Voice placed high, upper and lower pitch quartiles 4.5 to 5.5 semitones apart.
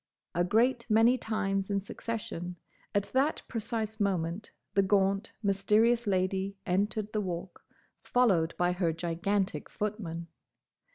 No: high, 200 Hz; average, 3.2 semitones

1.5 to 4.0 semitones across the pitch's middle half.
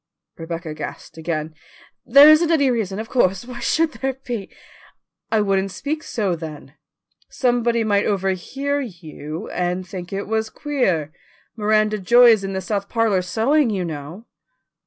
No: average, 5.2 semitones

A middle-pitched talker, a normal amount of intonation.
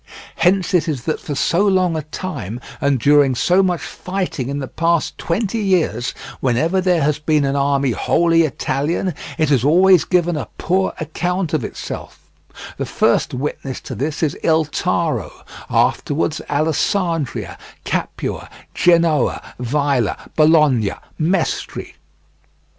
Yes: medium, 155 Hz; average, 4.0 semitones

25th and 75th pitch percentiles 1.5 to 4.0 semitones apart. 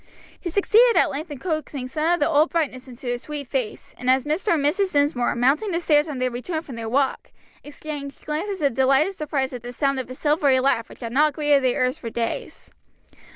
Yes: average, 3.3 semitones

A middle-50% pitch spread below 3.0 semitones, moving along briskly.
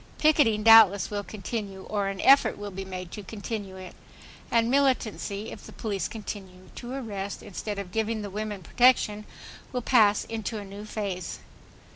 No: narrow, 2.4 semitones; average, 165 wpm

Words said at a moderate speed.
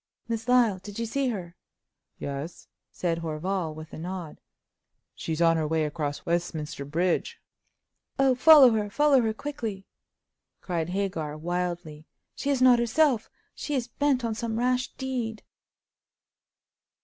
No: slow, 130 wpm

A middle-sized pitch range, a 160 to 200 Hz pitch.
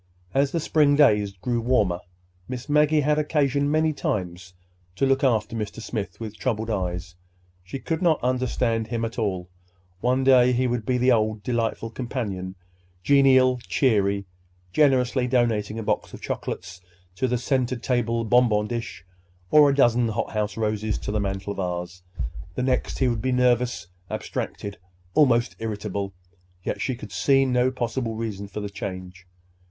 No: average, 3.9 semitones; low, 115 Hz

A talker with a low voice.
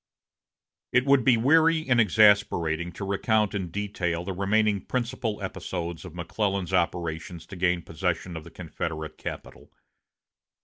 Yes: very low, 95 Hz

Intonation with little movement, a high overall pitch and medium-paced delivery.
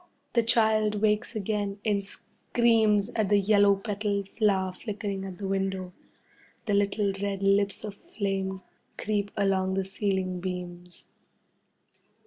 No: narrow, 1.6 semitones; high, 200 Hz; slow, 125 wpm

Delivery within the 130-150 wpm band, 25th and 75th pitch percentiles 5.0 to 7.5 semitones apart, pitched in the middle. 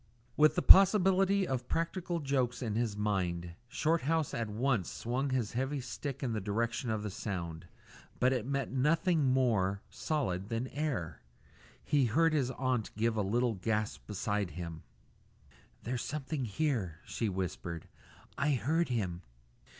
No: average, 145 wpm; wide, 5.6 semitones; low, 120 Hz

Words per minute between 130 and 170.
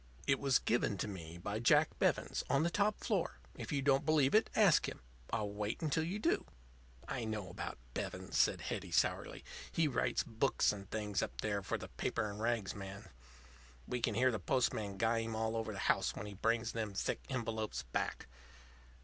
No: average, 195 wpm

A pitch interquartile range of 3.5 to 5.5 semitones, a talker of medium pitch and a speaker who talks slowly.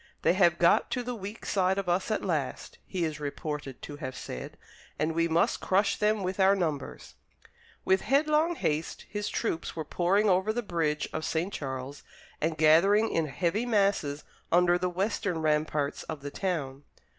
No: average, 4.8 semitones; medium, 175 Hz; average, 175 wpm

